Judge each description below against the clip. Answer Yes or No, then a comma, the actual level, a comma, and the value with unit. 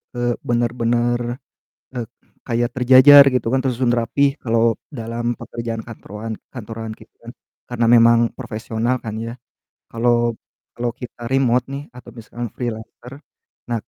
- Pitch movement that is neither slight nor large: No, narrow, 1.2 semitones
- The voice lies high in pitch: No, low, 120 Hz